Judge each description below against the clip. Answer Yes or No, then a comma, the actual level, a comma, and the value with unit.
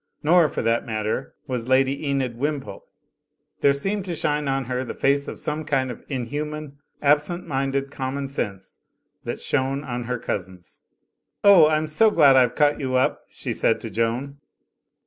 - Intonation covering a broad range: No, average, 3.1 semitones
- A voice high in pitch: No, low, 135 Hz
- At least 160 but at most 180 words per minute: Yes, average, 165 wpm